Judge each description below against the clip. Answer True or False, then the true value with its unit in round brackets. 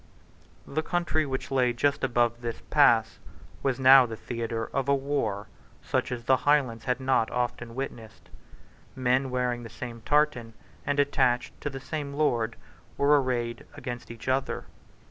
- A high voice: False (125 Hz)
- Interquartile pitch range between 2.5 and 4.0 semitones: True (2.8 semitones)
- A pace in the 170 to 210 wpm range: False (155 wpm)